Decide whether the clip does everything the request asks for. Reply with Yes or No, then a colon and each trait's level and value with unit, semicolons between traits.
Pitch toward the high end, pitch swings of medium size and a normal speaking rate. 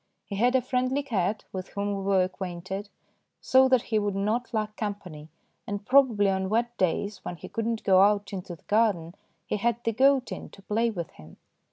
No: high, 205 Hz; average, 3.5 semitones; fast, 210 wpm